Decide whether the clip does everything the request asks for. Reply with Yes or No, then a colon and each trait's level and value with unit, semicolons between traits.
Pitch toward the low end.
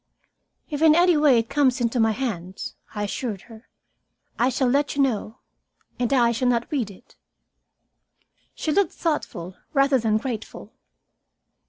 No: high, 245 Hz